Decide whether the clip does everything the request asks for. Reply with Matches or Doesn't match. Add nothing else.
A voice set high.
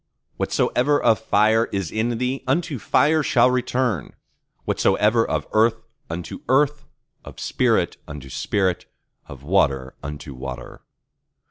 Doesn't match